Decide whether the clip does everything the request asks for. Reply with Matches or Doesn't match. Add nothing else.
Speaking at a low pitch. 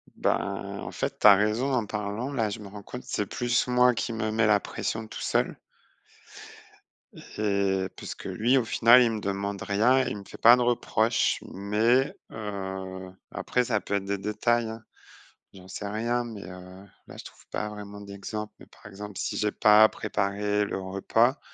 Matches